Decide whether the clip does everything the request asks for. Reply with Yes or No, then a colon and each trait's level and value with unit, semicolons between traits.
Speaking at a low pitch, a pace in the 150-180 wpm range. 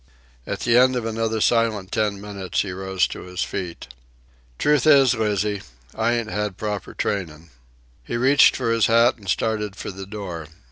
Yes: low, 105 Hz; average, 175 wpm